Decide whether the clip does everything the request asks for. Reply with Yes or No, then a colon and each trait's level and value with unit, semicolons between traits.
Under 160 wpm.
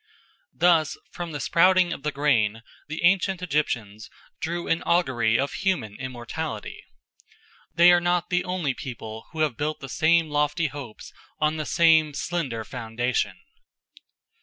Yes: average, 140 wpm